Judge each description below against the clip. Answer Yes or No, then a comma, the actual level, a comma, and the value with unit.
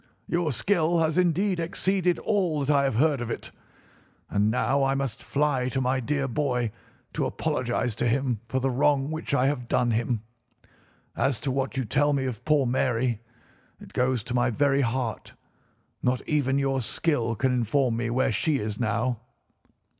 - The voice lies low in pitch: Yes, low, 130 Hz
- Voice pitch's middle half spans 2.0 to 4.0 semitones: Yes, average, 3.2 semitones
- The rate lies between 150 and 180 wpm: Yes, average, 175 wpm